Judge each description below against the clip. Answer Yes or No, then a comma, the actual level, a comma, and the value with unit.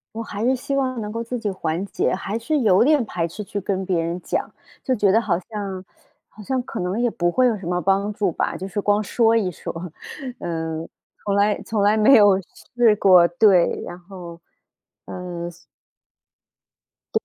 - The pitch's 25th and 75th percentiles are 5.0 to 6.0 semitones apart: No, average, 3.8 semitones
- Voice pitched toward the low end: No, high, 200 Hz